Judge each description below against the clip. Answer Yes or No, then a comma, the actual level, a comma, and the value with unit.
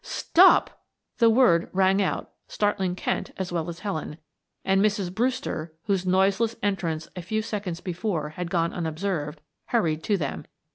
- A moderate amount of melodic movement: Yes, average, 3.6 semitones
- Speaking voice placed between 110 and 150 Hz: No, medium, 185 Hz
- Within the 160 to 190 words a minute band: No, average, 150 wpm